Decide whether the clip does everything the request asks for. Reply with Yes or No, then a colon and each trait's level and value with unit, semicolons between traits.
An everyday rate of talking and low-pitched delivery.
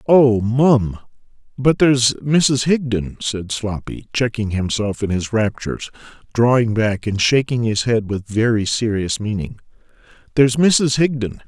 No: slow, 130 wpm; low, 115 Hz